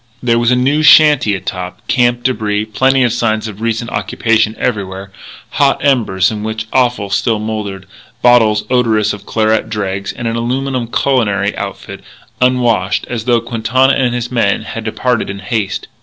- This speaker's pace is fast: No, average, 160 wpm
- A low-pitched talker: Yes, low, 115 Hz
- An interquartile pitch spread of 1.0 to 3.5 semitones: Yes, average, 2.8 semitones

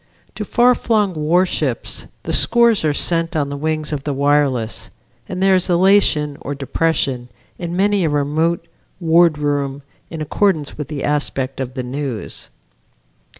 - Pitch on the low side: No, medium, 150 Hz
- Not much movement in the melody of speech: No, average, 3.6 semitones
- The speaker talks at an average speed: Yes, average, 150 wpm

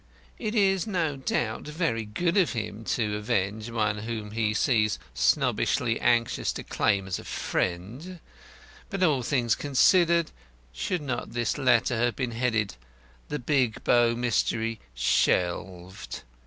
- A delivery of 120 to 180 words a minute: Yes, average, 140 wpm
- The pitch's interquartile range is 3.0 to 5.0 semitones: No, wide, 5.5 semitones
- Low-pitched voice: Yes, low, 120 Hz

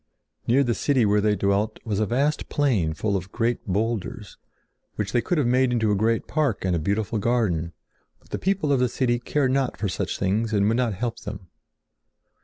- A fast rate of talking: Yes, fast, 210 wpm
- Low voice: Yes, low, 110 Hz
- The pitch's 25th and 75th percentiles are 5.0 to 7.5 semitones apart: No, average, 3.8 semitones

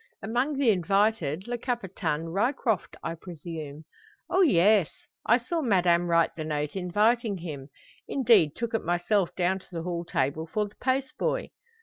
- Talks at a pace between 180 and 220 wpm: No, average, 155 wpm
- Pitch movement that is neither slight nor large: No, wide, 5.7 semitones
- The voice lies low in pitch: No, high, 190 Hz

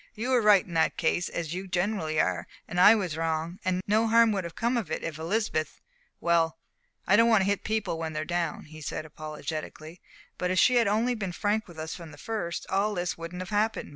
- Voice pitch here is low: No, medium, 180 Hz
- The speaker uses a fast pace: Yes, fast, 230 wpm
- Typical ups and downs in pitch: Yes, average, 4.7 semitones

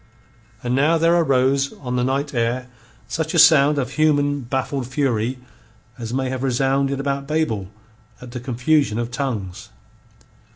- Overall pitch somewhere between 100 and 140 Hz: Yes, low, 135 Hz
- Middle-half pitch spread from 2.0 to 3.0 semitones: Yes, narrow, 2.5 semitones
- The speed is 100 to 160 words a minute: Yes, average, 150 wpm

